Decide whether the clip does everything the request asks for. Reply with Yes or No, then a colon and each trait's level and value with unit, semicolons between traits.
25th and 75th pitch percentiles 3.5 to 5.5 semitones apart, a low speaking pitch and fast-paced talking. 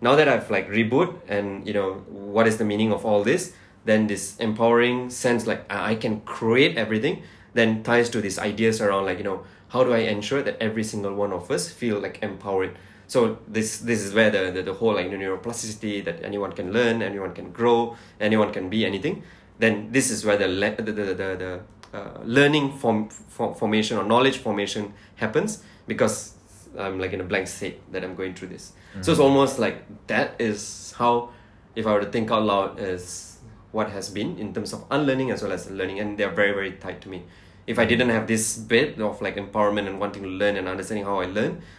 No: average, 2.7 semitones; low, 105 Hz; fast, 215 wpm